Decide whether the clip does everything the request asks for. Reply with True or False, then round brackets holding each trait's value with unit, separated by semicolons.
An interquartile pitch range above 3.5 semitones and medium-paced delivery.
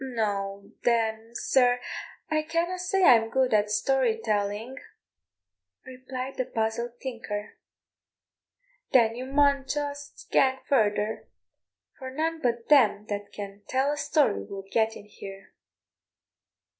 False (4.2 semitones; 120 wpm)